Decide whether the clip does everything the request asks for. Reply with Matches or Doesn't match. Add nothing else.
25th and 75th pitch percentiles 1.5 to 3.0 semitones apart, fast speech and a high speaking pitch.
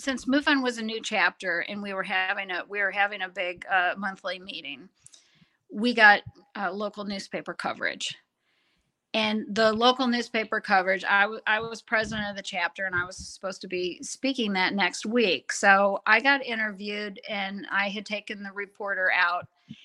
Doesn't match